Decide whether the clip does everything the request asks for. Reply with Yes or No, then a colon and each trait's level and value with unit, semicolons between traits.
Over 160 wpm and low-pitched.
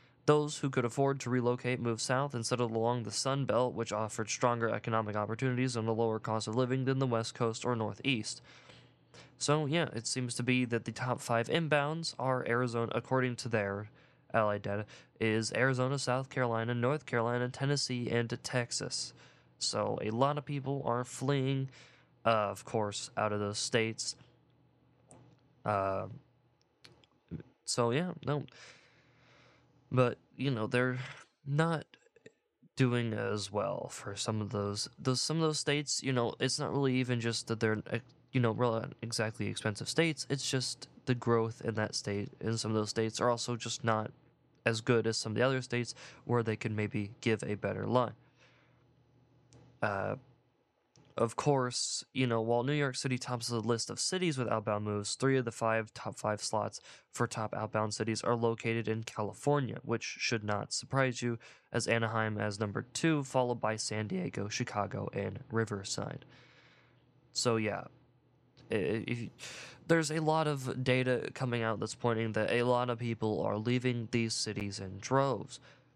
Yes: average, 170 wpm; low, 120 Hz